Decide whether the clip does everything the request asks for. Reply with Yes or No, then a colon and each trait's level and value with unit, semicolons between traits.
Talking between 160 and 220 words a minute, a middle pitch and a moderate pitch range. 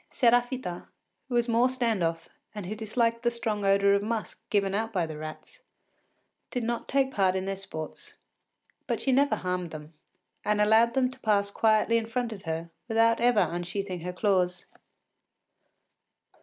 No: average, 170 wpm; high, 210 Hz; average, 4.2 semitones